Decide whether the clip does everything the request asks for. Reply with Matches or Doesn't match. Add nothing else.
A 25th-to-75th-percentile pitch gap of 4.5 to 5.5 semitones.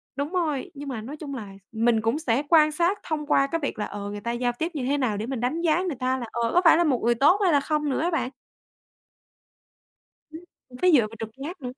Matches